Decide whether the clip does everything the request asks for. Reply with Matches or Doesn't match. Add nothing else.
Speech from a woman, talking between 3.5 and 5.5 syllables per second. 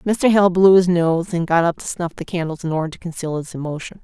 Doesn't match